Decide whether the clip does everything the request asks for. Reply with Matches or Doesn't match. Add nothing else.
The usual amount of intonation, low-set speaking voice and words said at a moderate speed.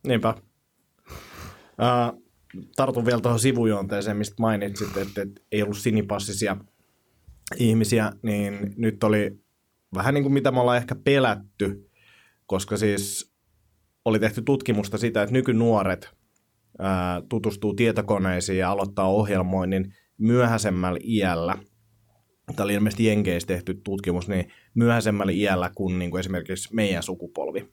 Matches